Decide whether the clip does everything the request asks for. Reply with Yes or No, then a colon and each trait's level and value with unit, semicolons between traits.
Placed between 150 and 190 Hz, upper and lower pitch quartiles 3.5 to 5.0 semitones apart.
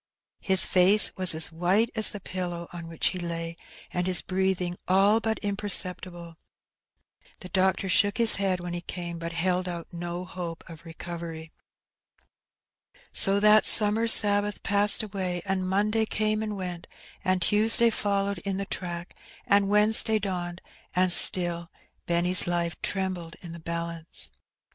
No: medium, 185 Hz; average, 2.9 semitones